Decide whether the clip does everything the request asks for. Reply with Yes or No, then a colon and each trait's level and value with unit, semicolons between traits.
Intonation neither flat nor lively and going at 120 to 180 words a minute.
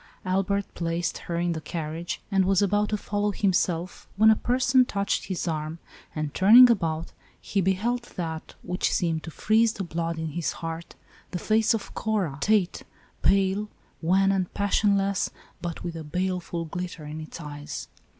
Yes: average, 3.6 semitones; average, 170 wpm